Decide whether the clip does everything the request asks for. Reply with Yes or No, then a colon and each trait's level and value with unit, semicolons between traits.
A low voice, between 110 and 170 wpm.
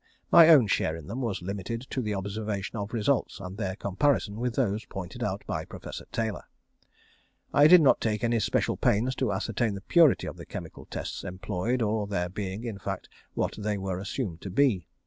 No: low, 105 Hz; average, 200 wpm